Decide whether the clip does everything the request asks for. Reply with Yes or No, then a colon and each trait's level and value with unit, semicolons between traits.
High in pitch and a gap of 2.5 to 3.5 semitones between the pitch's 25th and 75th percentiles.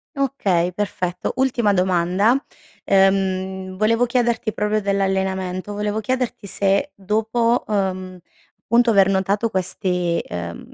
Yes: high, 195 Hz; average, 2.9 semitones